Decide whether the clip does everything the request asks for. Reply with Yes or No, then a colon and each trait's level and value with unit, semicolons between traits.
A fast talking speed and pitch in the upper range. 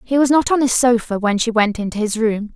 Yes: fast, 280 wpm; high, 230 Hz